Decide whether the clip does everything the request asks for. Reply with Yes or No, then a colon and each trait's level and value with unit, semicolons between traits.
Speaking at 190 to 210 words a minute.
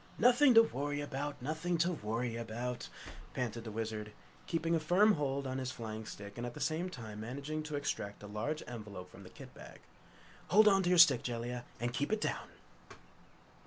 Yes: average, 195 wpm